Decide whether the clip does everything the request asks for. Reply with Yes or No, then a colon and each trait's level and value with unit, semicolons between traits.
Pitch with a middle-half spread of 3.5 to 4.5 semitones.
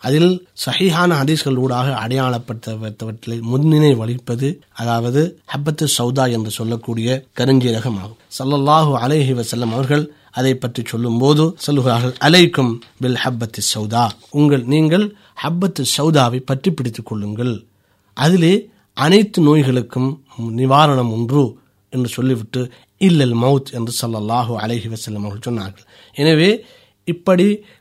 Yes: average, 4.2 semitones